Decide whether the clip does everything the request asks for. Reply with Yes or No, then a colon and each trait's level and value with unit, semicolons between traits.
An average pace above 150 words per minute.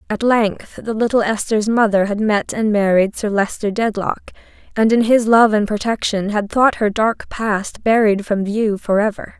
Yes: average, 185 wpm